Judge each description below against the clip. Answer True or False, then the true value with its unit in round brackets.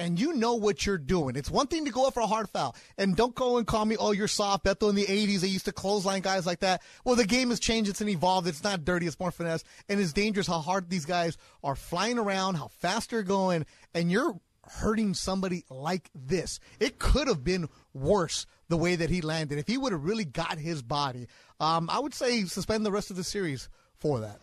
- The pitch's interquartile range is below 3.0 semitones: False (3.9 semitones)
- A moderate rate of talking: False (245 wpm)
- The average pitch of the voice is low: False (190 Hz)